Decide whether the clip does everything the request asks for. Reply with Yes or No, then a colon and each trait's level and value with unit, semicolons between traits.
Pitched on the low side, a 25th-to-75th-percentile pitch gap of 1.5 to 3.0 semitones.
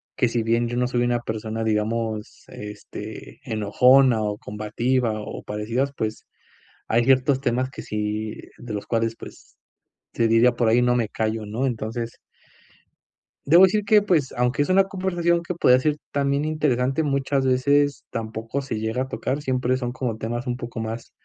No: low, 120 Hz; average, 3.5 semitones